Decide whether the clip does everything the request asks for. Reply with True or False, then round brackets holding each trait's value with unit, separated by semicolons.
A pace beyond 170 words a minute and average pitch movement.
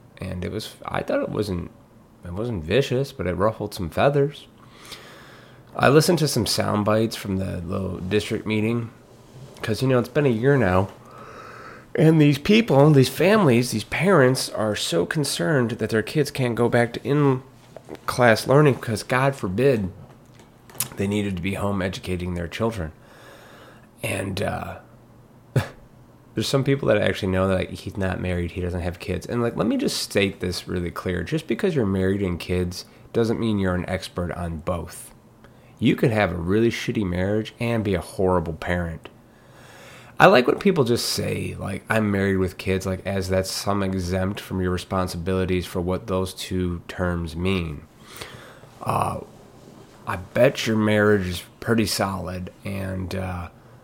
False (165 wpm; 4.5 semitones)